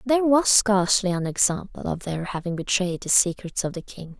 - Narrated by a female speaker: Yes, female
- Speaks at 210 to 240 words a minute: No, average, 200 wpm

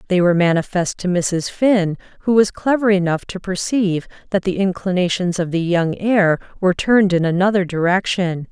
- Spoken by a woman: Yes, female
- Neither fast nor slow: Yes, average, 170 wpm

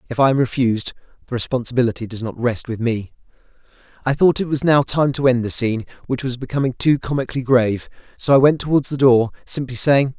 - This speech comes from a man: Yes, male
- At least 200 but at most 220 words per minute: Yes, fast, 205 wpm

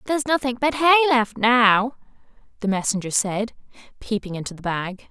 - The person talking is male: No, female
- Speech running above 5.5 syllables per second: No, 5.3 syllables/s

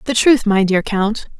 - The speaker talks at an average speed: No, fast, 215 wpm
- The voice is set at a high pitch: Yes, high, 215 Hz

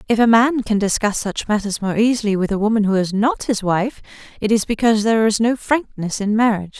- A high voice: Yes, high, 215 Hz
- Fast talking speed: Yes, fast, 230 wpm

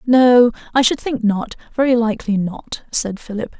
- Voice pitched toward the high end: Yes, high, 235 Hz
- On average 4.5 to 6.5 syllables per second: Yes, 4.7 syllables/s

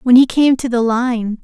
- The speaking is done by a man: No, female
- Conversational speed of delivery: No, fast, 250 wpm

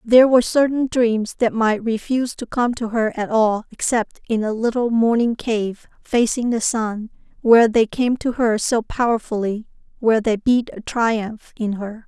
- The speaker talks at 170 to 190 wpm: Yes, average, 175 wpm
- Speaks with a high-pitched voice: Yes, high, 230 Hz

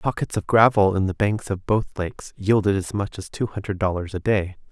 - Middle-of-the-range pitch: No, low, 100 Hz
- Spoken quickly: Yes, fast, 230 wpm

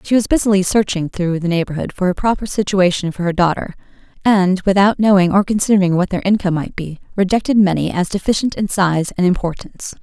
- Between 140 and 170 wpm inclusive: No, average, 190 wpm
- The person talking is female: Yes, female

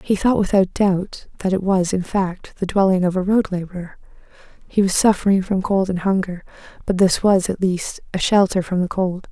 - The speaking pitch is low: No, high, 190 Hz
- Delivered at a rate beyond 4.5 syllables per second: Yes, 5.1 syllables/s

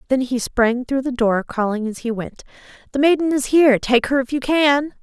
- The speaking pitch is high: Yes, very high, 255 Hz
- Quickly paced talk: Yes, fast, 225 wpm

